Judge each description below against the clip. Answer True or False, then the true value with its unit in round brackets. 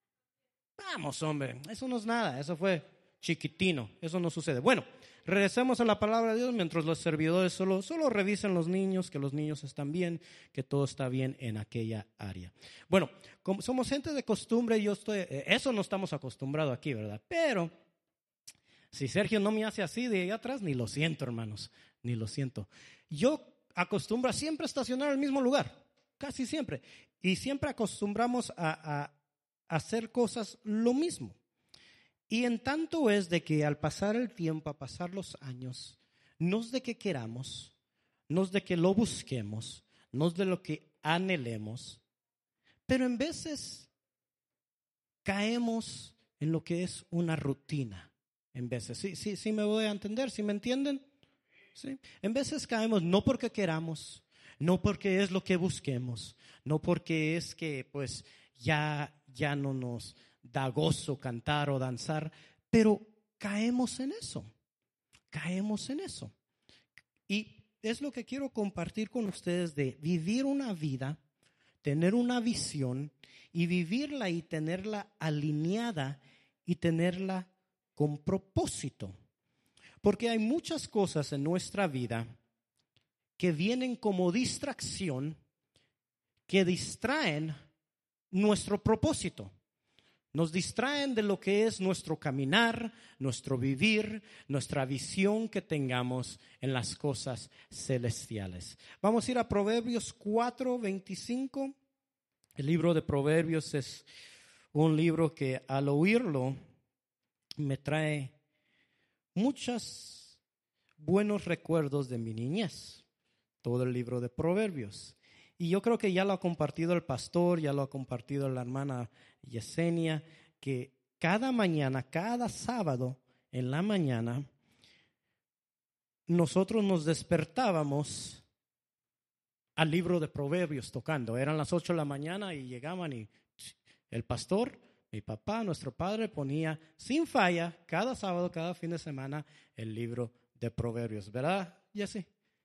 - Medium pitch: True (165 Hz)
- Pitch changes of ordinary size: False (7.5 semitones)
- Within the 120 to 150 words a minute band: True (140 wpm)